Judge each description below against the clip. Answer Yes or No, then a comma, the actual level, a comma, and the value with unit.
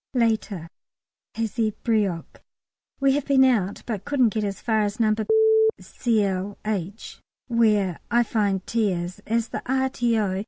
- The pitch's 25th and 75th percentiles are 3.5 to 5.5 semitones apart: No, average, 2.9 semitones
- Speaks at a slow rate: Yes, slow, 130 wpm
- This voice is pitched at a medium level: No, high, 215 Hz